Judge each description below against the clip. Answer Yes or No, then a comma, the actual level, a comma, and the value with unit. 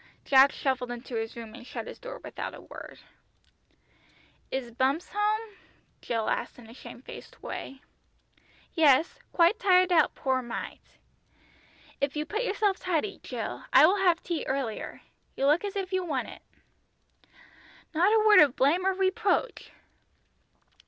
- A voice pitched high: Yes, very high, 315 Hz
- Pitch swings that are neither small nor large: No, wide, 6.8 semitones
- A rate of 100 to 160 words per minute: Yes, average, 150 wpm